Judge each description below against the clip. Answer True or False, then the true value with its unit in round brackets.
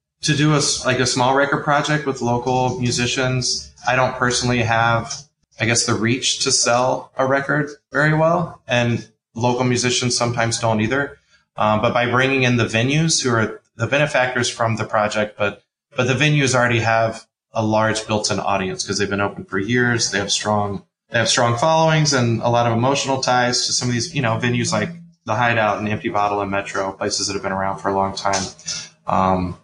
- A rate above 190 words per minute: True (200 wpm)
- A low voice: True (120 Hz)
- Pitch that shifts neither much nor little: True (3.1 semitones)